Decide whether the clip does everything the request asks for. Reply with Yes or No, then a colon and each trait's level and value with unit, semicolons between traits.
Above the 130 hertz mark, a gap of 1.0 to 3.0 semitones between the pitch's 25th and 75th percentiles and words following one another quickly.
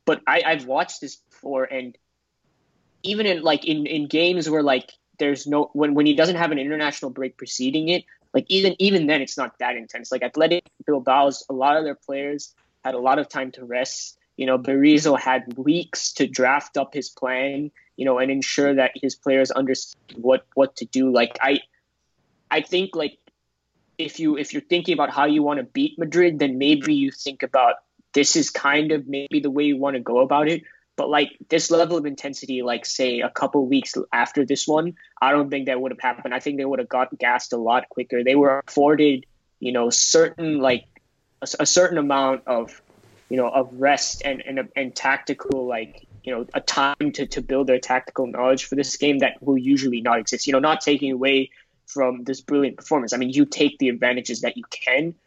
Yes: medium, 140 Hz; narrow, 2.5 semitones; fast, 215 wpm